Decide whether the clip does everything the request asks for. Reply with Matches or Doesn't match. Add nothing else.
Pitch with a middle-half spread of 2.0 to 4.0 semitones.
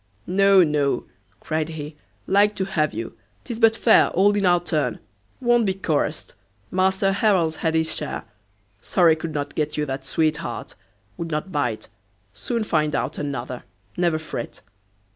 Doesn't match